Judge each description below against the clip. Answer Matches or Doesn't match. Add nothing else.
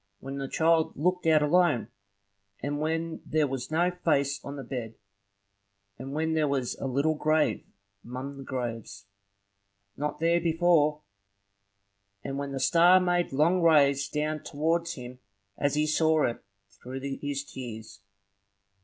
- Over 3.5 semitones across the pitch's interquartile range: Doesn't match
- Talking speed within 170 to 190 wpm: Doesn't match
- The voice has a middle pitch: Matches